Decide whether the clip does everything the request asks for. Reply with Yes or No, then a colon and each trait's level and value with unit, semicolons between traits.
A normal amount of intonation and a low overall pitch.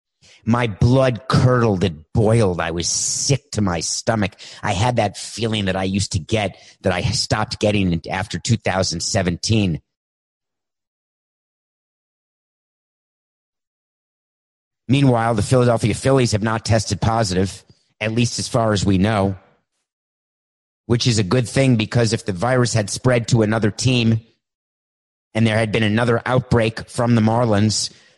Yes: average, 3.3 semitones; low, 110 Hz